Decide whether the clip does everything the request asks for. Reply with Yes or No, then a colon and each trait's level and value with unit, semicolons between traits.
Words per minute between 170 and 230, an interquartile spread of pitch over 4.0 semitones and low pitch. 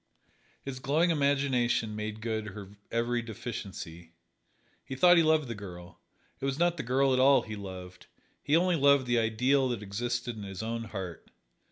Yes: average, 175 wpm; average, 4.7 semitones; low, 120 Hz